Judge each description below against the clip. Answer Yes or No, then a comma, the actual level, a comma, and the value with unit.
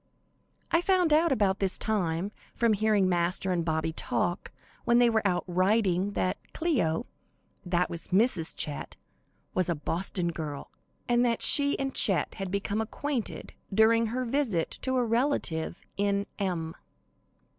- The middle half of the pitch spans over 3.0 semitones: Yes, average, 5.2 semitones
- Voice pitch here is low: No, high, 200 Hz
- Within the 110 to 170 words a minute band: Yes, average, 145 wpm